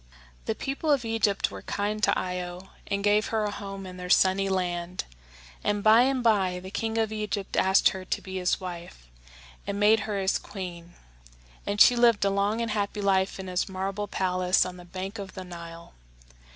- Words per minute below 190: No, average, 195 wpm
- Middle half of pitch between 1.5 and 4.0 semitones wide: Yes, narrow, 2.4 semitones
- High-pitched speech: Yes, high, 195 Hz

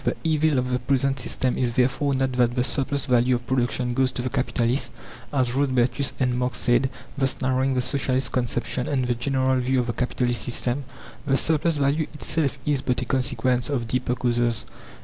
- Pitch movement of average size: No, narrow, 1.8 semitones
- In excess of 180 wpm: Yes, average, 190 wpm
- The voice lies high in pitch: No, low, 130 Hz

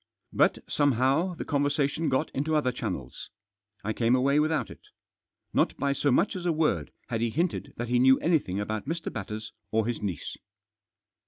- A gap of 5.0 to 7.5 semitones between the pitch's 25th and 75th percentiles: Yes, wide, 5.5 semitones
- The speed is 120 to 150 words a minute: No, average, 180 wpm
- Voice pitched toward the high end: No, low, 130 Hz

